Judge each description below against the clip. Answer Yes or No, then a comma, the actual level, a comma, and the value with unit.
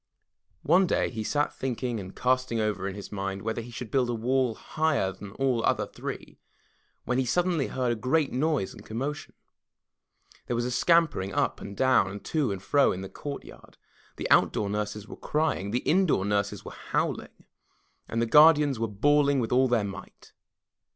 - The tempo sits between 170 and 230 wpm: Yes, average, 185 wpm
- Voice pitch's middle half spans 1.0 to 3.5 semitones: No, wide, 5.5 semitones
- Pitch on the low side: Yes, low, 120 Hz